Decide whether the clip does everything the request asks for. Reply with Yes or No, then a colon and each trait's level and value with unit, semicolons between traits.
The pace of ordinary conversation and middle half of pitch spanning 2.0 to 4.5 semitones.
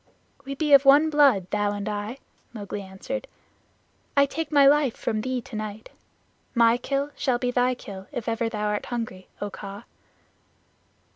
No: average, 155 wpm; average, 4.9 semitones